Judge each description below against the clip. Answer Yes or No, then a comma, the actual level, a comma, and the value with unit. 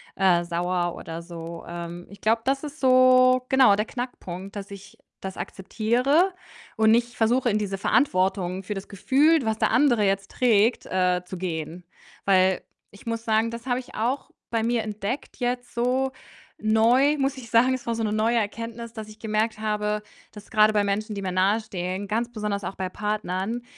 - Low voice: No, high, 215 Hz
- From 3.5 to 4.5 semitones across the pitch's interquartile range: Yes, average, 3.8 semitones